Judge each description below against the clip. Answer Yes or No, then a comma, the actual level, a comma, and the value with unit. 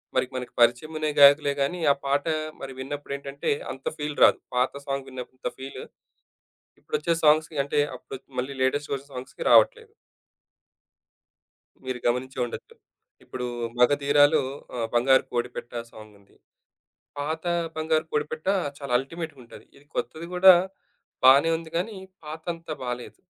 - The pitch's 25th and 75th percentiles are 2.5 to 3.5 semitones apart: Yes, average, 3.2 semitones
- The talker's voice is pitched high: No, medium, 140 Hz